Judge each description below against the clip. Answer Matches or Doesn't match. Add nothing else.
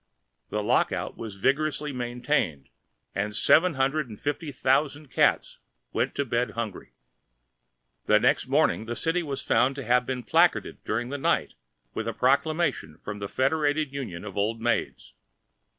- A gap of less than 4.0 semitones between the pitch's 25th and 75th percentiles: Doesn't match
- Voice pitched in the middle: Doesn't match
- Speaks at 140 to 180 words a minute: Matches